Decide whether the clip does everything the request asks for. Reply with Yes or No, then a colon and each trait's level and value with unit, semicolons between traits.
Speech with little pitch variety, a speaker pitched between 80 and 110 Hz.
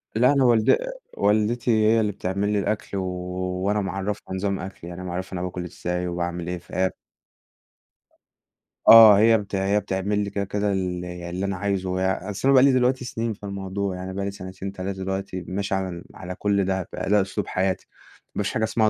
Yes: narrow, 2.1 semitones; low, 100 Hz